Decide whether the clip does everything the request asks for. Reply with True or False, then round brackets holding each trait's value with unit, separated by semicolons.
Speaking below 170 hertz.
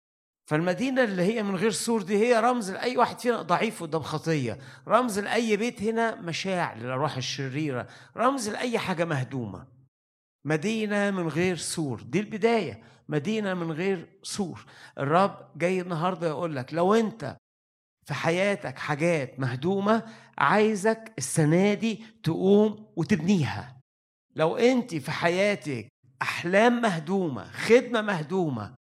False (175 Hz)